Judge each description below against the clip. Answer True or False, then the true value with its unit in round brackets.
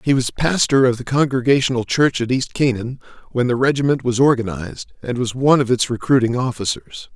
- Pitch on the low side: True (125 Hz)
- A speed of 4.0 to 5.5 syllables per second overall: False (5.7 syllables/s)